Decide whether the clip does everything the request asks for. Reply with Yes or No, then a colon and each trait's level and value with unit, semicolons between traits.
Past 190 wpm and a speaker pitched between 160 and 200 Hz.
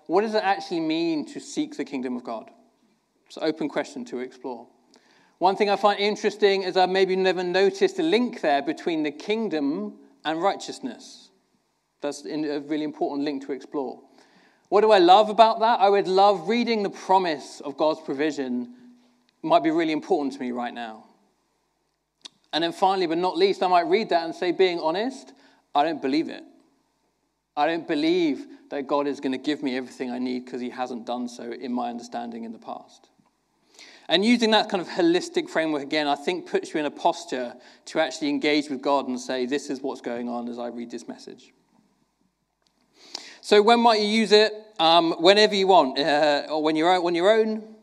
Yes: average, 200 wpm; high, 190 Hz